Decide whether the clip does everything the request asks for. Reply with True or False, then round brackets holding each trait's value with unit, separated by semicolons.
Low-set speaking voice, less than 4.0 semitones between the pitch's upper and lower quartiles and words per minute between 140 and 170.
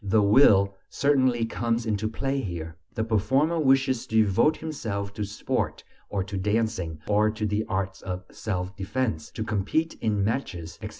True (105 Hz; 3.6 semitones; 165 wpm)